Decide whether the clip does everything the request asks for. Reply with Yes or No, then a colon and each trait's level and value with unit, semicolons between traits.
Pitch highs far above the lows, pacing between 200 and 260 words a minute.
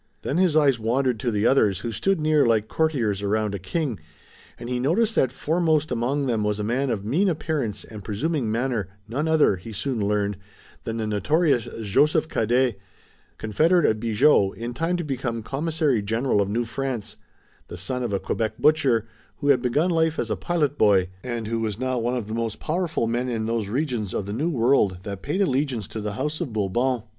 Yes: wide, 5.7 semitones; fast, 205 wpm